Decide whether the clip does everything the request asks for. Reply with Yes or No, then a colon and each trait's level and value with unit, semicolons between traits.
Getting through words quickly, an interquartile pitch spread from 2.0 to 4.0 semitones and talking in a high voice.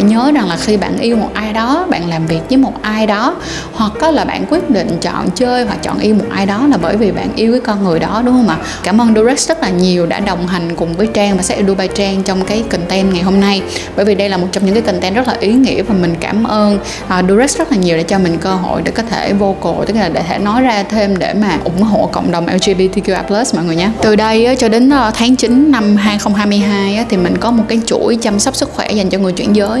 Yes: fast, 270 wpm; average, 3.4 semitones; high, 210 Hz